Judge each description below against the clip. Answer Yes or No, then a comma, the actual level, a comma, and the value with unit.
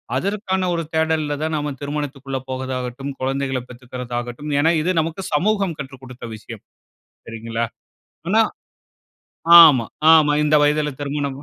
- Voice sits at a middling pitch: Yes, medium, 145 Hz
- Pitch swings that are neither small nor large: Yes, average, 3.8 semitones